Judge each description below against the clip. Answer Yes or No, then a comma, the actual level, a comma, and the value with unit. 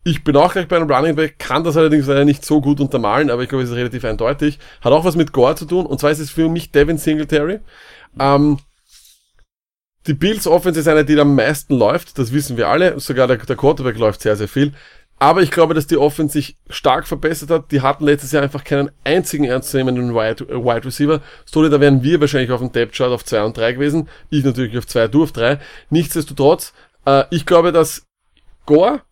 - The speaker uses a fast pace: Yes, fast, 225 wpm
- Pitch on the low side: No, medium, 145 Hz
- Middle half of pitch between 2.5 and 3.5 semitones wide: Yes, average, 2.9 semitones